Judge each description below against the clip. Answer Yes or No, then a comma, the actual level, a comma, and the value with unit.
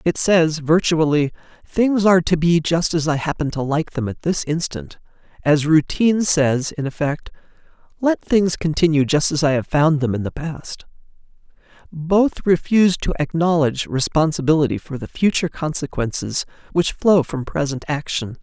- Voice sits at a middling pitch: Yes, medium, 160 Hz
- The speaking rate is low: No, average, 155 wpm